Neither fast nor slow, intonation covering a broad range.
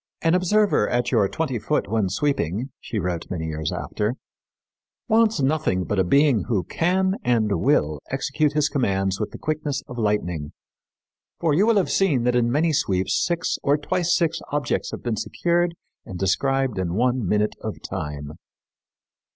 Yes: average, 165 wpm; wide, 8.1 semitones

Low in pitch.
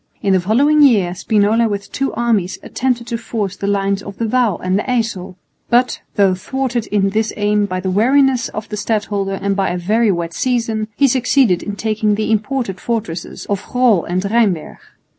No: high, 210 Hz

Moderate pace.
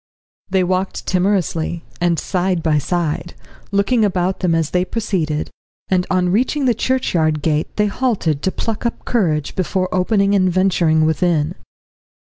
Yes: average, 145 wpm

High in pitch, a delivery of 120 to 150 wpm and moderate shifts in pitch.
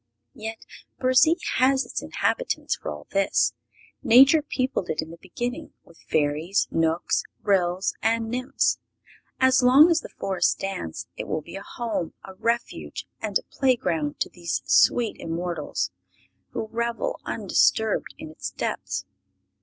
No: high, 215 Hz; average, 140 wpm; wide, 7.0 semitones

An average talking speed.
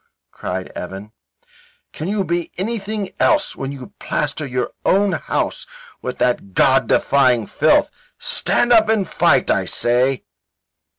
No: slow, 130 wpm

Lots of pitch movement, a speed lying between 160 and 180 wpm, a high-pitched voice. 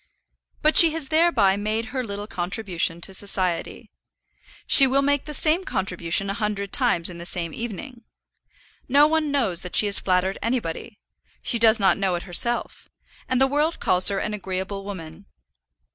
Yes: wide, 6.0 semitones; average, 170 wpm; high, 205 Hz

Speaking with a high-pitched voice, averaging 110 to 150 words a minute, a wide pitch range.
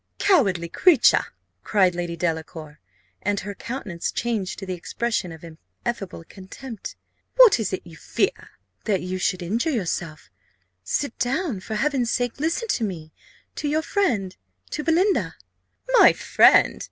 Yes: high, 205 Hz; average, 140 wpm; wide, 7.5 semitones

